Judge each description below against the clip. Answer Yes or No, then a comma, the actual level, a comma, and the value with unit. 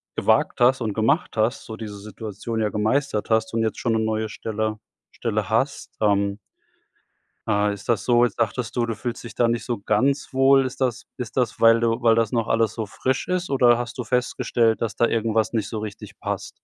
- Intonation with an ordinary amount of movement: No, narrow, 2.0 semitones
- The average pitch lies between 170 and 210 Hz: No, low, 115 Hz